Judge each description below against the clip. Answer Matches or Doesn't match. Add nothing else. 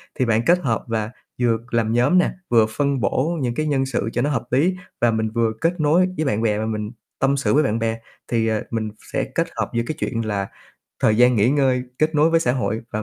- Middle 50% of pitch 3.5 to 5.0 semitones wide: Matches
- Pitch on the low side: Matches